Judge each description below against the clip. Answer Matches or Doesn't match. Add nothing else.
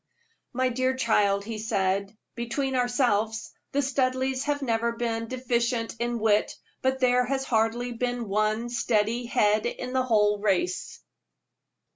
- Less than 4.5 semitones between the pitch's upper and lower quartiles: Matches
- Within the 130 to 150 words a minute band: Matches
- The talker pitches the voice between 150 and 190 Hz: Doesn't match